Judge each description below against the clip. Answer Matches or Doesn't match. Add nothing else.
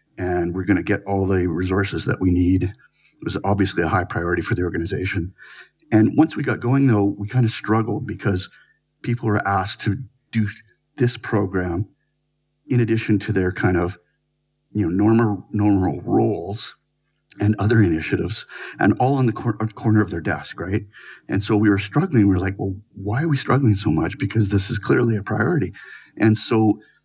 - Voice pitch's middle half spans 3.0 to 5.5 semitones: Matches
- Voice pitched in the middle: Doesn't match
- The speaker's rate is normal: Matches